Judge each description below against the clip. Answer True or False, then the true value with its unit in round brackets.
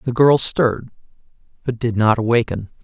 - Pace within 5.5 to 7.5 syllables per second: False (5.3 syllables/s)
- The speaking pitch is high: False (120 Hz)